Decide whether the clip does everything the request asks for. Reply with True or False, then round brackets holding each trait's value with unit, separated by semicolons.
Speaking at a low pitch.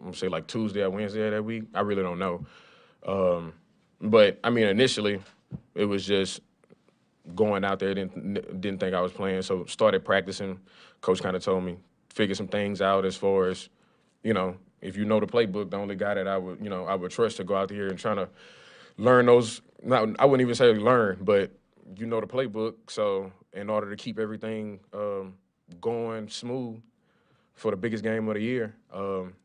True (100 Hz)